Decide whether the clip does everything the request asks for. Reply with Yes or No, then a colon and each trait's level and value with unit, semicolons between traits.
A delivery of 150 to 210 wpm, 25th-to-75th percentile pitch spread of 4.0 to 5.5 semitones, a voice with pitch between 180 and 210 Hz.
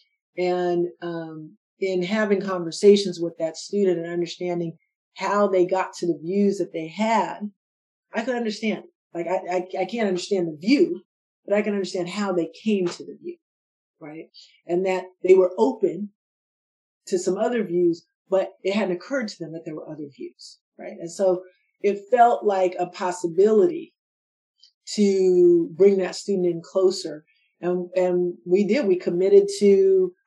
No: average, 165 wpm; average, 2.9 semitones; medium, 185 Hz